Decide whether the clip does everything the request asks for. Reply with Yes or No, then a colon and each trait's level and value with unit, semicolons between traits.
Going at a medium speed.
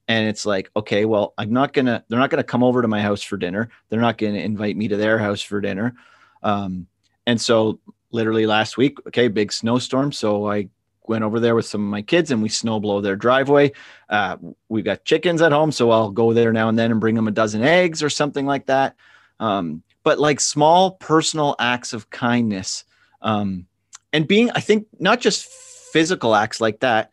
No: fast, 210 wpm